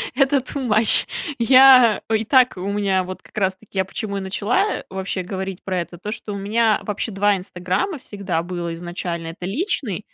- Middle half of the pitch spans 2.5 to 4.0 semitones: Yes, average, 3.4 semitones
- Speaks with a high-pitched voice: Yes, high, 200 Hz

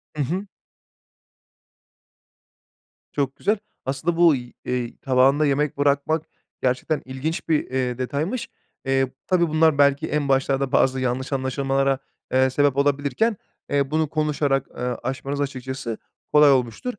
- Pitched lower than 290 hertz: Yes, medium, 140 Hz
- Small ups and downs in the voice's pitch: Yes, narrow, 2.3 semitones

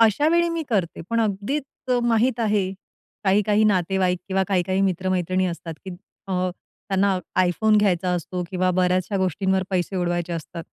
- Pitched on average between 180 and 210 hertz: Yes, high, 190 Hz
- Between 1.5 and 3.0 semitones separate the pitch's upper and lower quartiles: Yes, average, 2.7 semitones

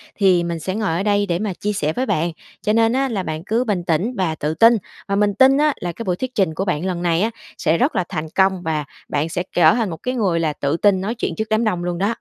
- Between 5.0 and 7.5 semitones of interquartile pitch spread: No, average, 4.4 semitones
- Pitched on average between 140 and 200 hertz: Yes, high, 190 Hz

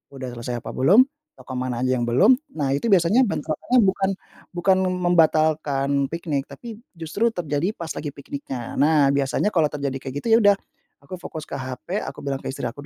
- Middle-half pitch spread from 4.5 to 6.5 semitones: Yes, average, 5.0 semitones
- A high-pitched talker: No, medium, 150 Hz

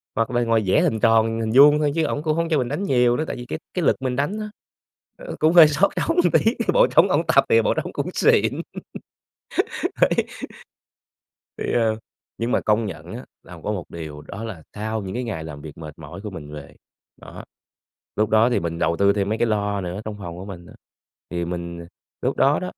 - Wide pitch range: Yes, wide, 6.9 semitones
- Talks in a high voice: No, low, 110 Hz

